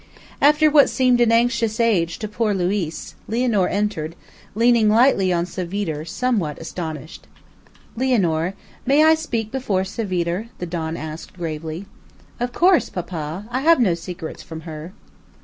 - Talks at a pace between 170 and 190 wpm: No, average, 140 wpm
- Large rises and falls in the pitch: Yes, wide, 6.1 semitones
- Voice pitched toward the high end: Yes, high, 195 Hz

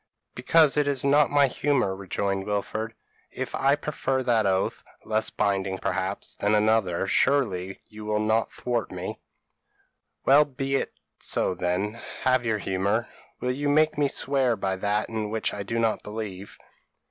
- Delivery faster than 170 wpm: No, average, 160 wpm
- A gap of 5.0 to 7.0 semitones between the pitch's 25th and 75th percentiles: Yes, average, 5.3 semitones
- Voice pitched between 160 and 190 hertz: No, low, 110 Hz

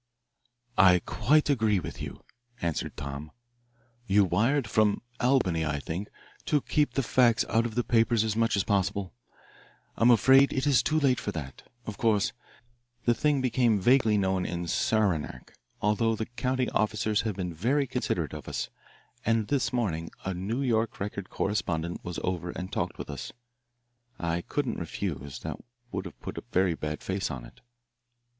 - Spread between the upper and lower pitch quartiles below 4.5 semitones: No, average, 5.1 semitones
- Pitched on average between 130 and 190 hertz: No, low, 105 Hz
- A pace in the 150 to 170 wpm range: Yes, average, 165 wpm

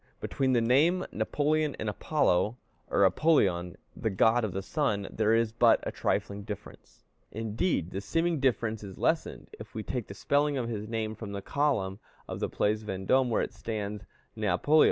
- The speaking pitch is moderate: No, low, 110 Hz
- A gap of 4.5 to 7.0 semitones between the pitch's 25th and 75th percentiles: Yes, average, 5.1 semitones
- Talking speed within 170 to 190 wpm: Yes, average, 175 wpm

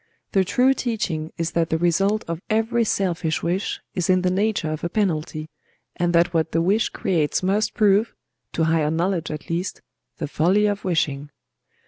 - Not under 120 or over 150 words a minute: No, average, 165 wpm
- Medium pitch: Yes, medium, 175 Hz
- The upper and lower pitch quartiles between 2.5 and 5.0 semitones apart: Yes, average, 3.8 semitones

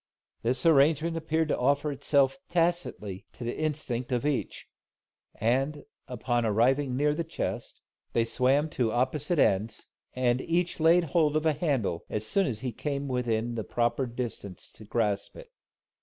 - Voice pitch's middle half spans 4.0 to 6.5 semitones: Yes, average, 4.6 semitones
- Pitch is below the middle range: Yes, low, 130 Hz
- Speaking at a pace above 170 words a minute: No, average, 155 wpm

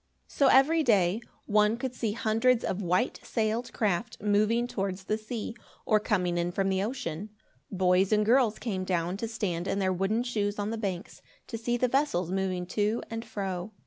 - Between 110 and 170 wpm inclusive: No, average, 185 wpm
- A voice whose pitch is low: No, high, 210 Hz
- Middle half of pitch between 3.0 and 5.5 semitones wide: Yes, average, 3.4 semitones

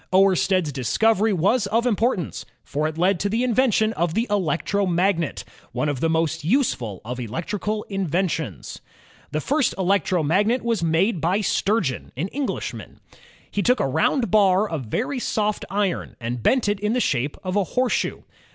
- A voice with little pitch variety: No, average, 5.2 semitones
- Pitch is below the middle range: No, high, 195 Hz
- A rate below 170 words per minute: Yes, average, 160 wpm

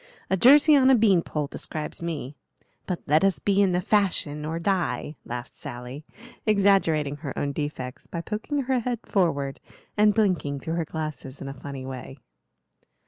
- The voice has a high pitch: No, medium, 165 Hz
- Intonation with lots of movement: Yes, wide, 5.9 semitones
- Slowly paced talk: No, average, 170 wpm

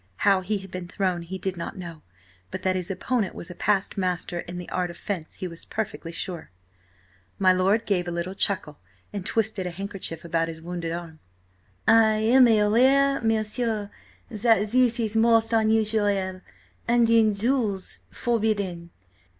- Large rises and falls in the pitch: No, average, 3.8 semitones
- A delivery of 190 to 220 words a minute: No, average, 160 wpm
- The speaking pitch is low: No, high, 200 Hz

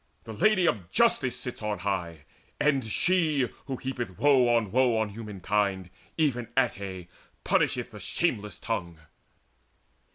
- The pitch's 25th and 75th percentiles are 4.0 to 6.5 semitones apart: Yes, average, 5.1 semitones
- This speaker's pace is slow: Yes, slow, 130 wpm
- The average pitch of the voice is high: No, low, 110 Hz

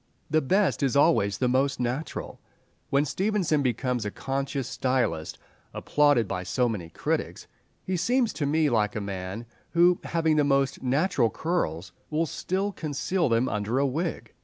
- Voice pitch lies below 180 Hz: Yes, medium, 140 Hz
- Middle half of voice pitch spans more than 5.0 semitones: Yes, wide, 5.5 semitones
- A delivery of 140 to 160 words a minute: Yes, average, 155 wpm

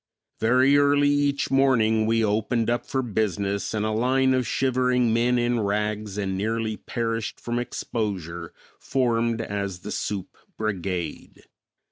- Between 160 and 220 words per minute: No, slow, 135 wpm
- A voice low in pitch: Yes, low, 115 Hz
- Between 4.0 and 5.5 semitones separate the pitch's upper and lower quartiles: No, average, 3.3 semitones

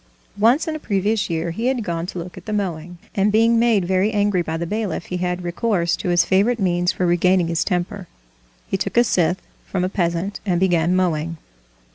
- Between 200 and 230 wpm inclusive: Yes, fast, 205 wpm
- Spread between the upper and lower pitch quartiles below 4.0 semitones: Yes, average, 3.2 semitones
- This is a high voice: No, medium, 180 Hz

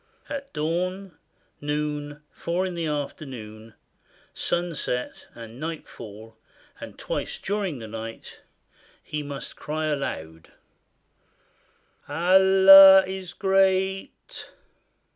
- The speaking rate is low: Yes, slow, 90 wpm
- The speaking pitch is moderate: Yes, medium, 155 Hz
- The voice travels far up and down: Yes, wide, 5.7 semitones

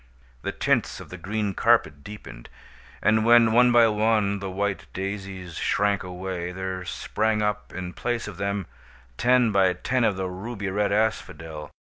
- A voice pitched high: No, low, 100 Hz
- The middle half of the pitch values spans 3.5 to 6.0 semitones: No, average, 2.9 semitones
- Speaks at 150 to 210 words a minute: Yes, average, 160 wpm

